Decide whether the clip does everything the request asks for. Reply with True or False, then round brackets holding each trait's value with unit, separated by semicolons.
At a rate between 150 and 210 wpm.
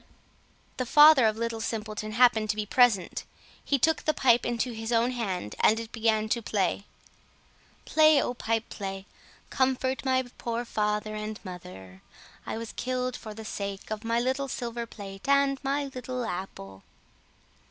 True (160 wpm)